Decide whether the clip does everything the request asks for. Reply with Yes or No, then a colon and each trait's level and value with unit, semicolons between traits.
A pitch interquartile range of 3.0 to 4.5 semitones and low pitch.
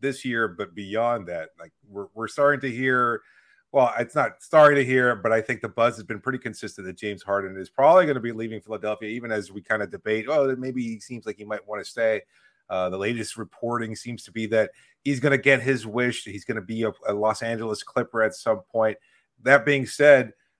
Yes: average, 3.4 semitones; low, 115 Hz